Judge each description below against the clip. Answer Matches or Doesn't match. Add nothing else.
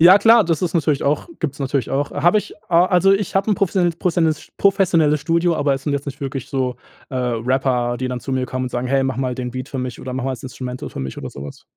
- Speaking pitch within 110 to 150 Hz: Matches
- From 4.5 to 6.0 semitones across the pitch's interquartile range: Matches